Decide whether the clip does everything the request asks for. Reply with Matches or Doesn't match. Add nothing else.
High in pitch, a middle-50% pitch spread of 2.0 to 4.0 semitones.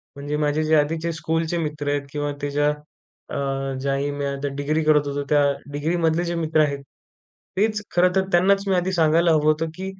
Doesn't match